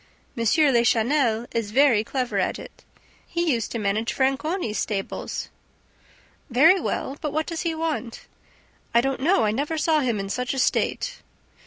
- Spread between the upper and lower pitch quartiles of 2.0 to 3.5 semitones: No, average, 5.2 semitones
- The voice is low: No, very high, 265 Hz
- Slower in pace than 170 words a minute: Yes, average, 160 wpm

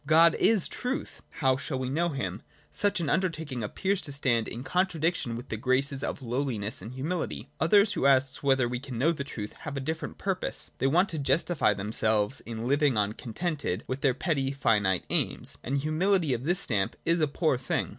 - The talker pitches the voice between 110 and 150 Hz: Yes, medium, 140 Hz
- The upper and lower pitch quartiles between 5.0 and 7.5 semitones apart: Yes, average, 5.3 semitones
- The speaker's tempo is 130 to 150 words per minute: No, average, 200 wpm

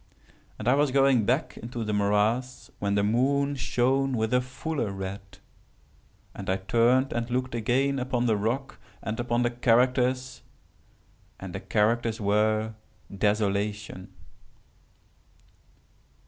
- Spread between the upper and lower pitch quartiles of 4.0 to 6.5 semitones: No, average, 3.4 semitones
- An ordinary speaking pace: No, slow, 125 wpm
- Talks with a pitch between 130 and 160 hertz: No, low, 120 Hz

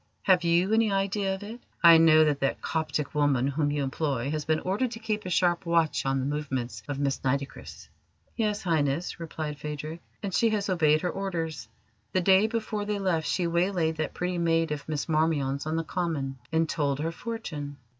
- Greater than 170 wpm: Yes, average, 195 wpm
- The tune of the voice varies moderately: Yes, average, 4.2 semitones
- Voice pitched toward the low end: No, medium, 160 Hz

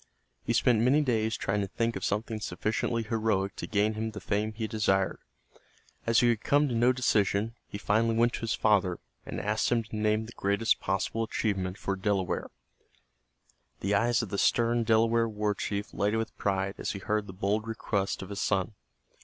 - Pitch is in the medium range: No, low, 110 Hz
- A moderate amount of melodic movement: No, narrow, 2.2 semitones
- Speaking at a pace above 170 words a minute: Yes, average, 195 wpm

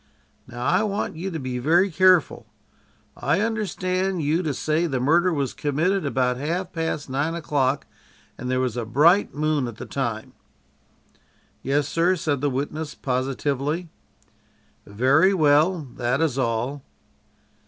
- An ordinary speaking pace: Yes, average, 145 wpm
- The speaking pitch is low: No, medium, 150 Hz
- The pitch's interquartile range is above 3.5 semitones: Yes, average, 4.7 semitones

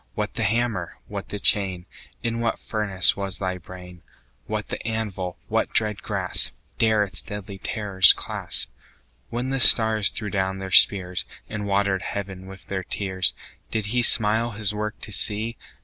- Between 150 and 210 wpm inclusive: Yes, average, 165 wpm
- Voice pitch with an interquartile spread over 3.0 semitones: No, narrow, 2.6 semitones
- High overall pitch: No, low, 100 Hz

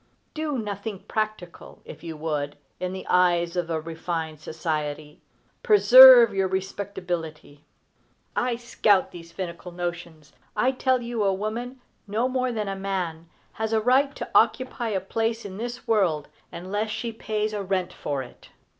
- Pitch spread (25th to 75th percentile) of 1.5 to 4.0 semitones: No, average, 5.0 semitones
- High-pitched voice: Yes, high, 195 Hz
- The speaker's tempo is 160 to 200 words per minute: No, average, 150 wpm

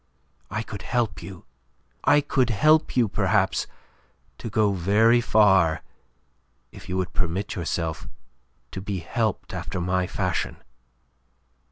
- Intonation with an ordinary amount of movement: Yes, average, 3.7 semitones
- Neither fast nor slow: No, slow, 125 wpm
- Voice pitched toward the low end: Yes, low, 100 Hz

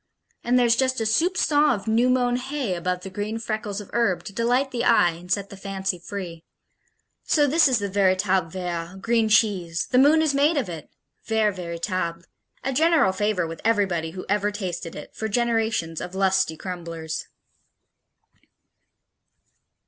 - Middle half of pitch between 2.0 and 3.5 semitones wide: No, average, 4.9 semitones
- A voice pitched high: Yes, high, 205 Hz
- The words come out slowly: No, average, 165 wpm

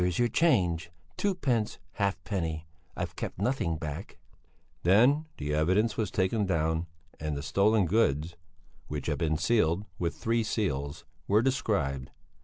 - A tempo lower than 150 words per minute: Yes, average, 140 wpm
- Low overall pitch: Yes, very low, 95 Hz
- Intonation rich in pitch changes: Yes, wide, 5.9 semitones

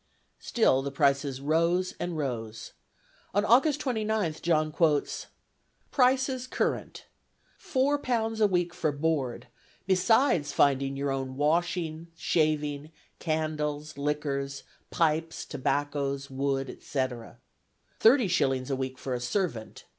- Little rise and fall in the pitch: No, average, 4.9 semitones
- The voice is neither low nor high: Yes, medium, 155 Hz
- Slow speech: Yes, slow, 115 wpm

